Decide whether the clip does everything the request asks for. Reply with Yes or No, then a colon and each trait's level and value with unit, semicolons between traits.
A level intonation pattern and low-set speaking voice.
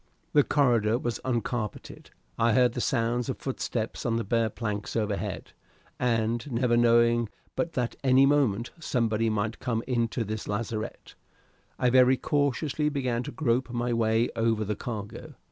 Yes: narrow, 2.1 semitones; low, 120 Hz